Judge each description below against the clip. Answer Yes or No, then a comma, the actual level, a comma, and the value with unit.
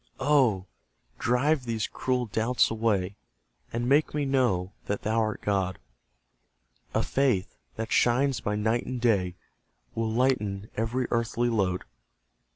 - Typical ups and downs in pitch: Yes, average, 3.5 semitones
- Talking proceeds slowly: Yes, slow, 130 wpm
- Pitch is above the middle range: No, low, 115 Hz